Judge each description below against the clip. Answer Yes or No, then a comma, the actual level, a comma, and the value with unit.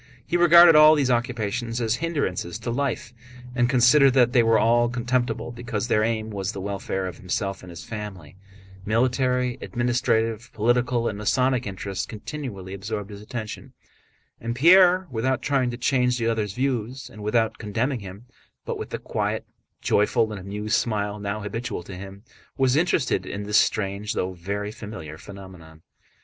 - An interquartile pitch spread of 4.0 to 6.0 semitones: No, average, 3.6 semitones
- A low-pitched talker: Yes, low, 115 Hz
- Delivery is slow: No, average, 160 wpm